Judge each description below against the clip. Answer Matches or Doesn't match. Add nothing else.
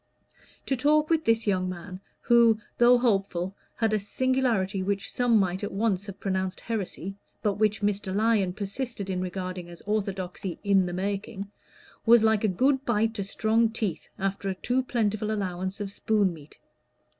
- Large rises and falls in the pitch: Doesn't match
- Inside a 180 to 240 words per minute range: Doesn't match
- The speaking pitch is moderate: Doesn't match